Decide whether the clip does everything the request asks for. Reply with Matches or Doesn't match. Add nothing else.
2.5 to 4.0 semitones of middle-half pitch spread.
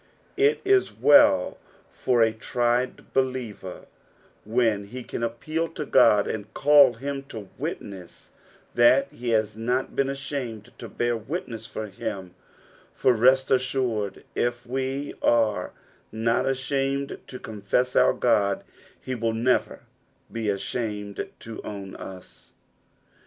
Matches